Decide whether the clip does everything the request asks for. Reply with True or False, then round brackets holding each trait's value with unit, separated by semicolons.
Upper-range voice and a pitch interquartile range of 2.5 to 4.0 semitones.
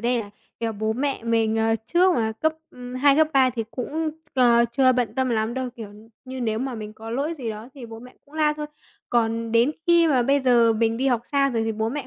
True (245 Hz; 3.4 semitones)